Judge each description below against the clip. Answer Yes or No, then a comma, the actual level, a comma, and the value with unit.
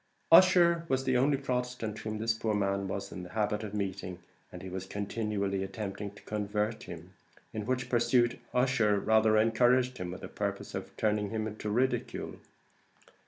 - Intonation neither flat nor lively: Yes, average, 3.6 semitones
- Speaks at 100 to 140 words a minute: No, average, 170 wpm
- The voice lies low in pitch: Yes, low, 110 Hz